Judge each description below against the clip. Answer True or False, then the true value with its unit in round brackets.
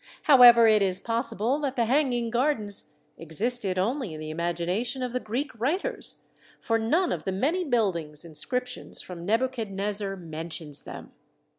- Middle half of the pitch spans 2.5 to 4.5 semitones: False (5.3 semitones)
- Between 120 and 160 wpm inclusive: True (155 wpm)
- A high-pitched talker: True (225 Hz)